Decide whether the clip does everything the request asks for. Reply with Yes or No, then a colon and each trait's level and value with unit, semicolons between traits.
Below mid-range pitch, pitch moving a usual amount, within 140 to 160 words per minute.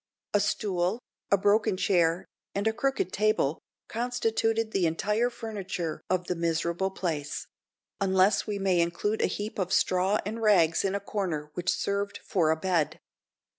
No: high, 195 Hz; average, 3.4 semitones; average, 155 wpm